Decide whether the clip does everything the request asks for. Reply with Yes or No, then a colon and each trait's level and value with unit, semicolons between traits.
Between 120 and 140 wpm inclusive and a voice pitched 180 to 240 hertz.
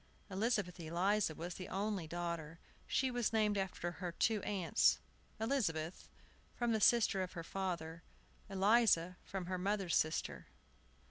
Yes: slow, 135 wpm; high, 190 Hz